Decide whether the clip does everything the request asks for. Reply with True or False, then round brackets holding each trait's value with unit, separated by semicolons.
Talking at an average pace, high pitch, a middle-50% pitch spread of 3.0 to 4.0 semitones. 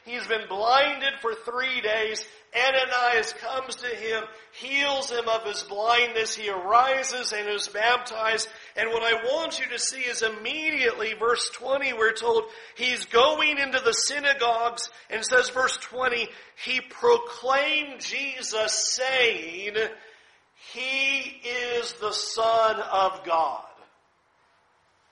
False (125 wpm; 240 Hz; 3.3 semitones)